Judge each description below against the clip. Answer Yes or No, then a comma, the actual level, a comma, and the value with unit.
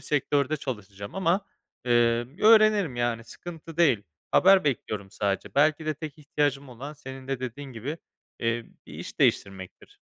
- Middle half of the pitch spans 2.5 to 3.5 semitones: No, average, 4.9 semitones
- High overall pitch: No, low, 135 Hz